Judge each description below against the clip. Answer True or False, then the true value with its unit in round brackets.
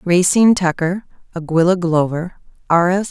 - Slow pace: True (115 wpm)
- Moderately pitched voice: True (175 Hz)